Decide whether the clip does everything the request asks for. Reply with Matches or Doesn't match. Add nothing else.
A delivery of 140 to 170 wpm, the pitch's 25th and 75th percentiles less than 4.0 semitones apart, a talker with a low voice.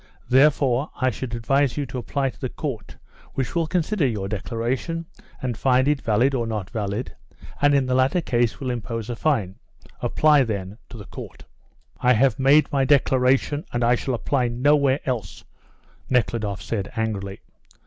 Matches